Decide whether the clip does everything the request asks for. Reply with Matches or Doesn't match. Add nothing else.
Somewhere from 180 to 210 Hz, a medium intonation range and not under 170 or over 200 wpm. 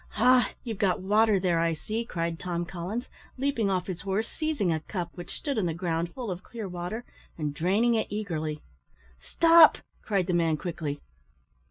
Matches